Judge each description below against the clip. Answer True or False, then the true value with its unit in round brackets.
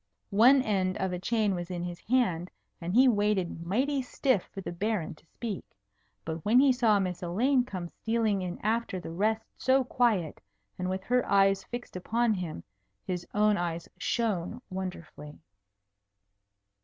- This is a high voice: True (200 Hz)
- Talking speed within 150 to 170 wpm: True (160 wpm)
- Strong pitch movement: False (4.7 semitones)